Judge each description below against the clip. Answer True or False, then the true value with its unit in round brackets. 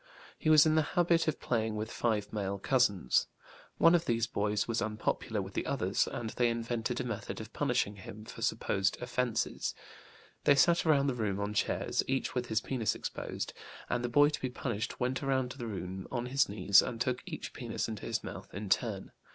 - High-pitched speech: False (120 Hz)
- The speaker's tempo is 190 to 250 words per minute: True (200 wpm)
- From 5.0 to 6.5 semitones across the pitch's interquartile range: False (4.0 semitones)